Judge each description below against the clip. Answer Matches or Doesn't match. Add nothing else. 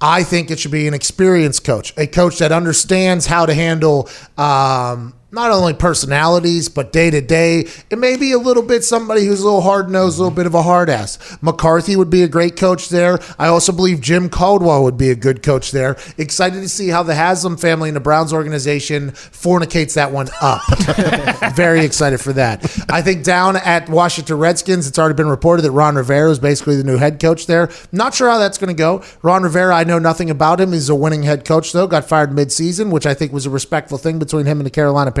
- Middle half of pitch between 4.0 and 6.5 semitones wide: Doesn't match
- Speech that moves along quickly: Matches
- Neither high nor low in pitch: Matches